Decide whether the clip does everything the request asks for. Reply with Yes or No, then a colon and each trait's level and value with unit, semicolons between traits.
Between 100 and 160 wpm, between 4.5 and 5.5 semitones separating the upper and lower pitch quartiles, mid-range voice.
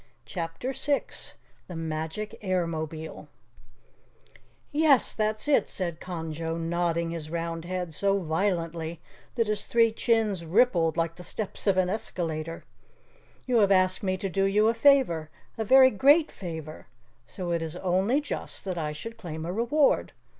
Yes: average, 150 wpm; average, 4.8 semitones; medium, 180 Hz